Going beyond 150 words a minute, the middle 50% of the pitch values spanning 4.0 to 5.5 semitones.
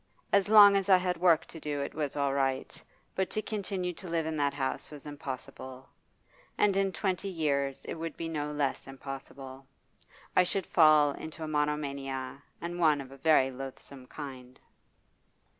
Yes: average, 175 wpm; average, 4.3 semitones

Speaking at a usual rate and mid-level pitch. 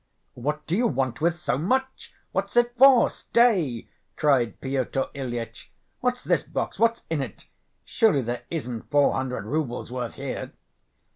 Yes: average, 150 wpm; medium, 145 Hz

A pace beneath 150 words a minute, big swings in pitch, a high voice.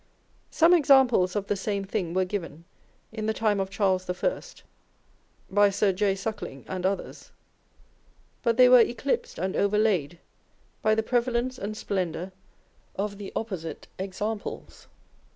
No: average, 140 wpm; average, 2.9 semitones; high, 205 Hz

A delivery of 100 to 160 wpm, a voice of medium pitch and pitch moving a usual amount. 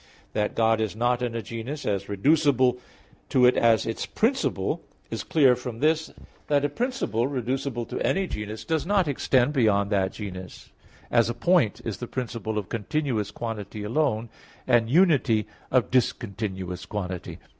No: average, 155 wpm; low, 120 Hz; average, 4.6 semitones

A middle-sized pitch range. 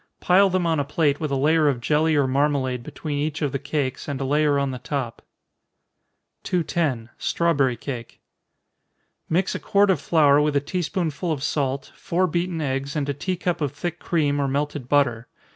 Yes: average, 3.0 semitones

